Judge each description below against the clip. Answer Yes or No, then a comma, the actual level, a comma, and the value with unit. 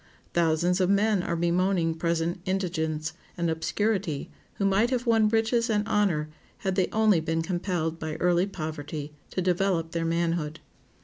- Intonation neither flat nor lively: Yes, average, 3.3 semitones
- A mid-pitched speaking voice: Yes, medium, 175 Hz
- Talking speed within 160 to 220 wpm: No, average, 150 wpm